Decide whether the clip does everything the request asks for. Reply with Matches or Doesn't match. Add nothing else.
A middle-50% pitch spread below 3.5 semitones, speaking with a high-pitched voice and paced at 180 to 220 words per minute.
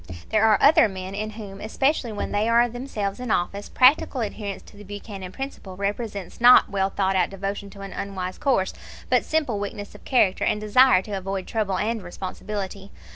Matches